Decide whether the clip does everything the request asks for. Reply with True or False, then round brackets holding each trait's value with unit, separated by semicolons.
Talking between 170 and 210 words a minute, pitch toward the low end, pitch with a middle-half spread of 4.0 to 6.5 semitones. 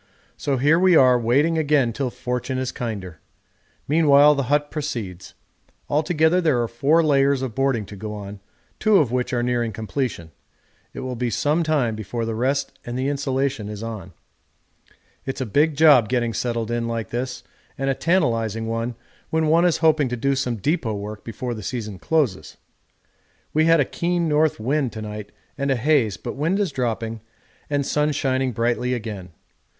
True (180 wpm; 130 Hz; 4.5 semitones)